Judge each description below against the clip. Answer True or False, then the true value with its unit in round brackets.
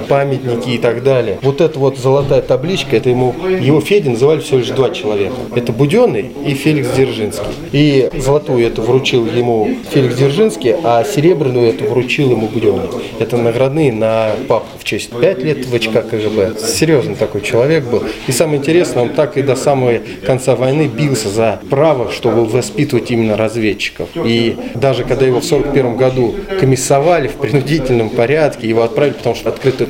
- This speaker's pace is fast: True (170 wpm)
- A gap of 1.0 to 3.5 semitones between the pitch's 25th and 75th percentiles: True (3.2 semitones)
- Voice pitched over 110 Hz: True (130 Hz)